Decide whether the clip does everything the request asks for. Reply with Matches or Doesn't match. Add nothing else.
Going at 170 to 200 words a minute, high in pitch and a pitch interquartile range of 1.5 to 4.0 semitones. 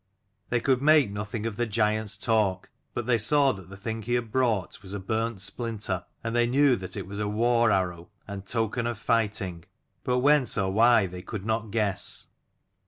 Doesn't match